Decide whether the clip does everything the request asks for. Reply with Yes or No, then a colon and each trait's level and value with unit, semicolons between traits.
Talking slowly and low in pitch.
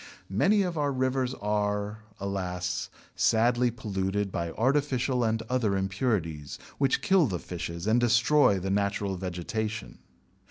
Yes: slow, 125 wpm; low, 105 Hz